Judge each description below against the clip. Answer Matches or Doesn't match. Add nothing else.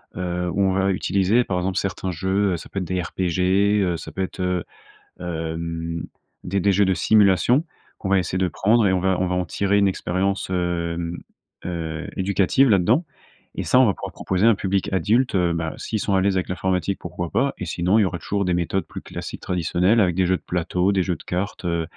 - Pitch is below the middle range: Matches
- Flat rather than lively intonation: Matches